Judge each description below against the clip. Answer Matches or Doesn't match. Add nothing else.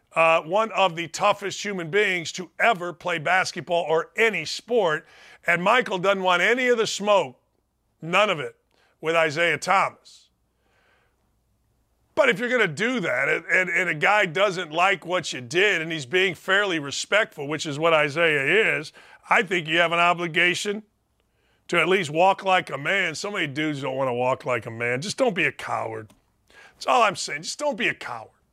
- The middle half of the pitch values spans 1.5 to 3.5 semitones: Doesn't match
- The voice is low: Doesn't match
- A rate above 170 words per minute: Matches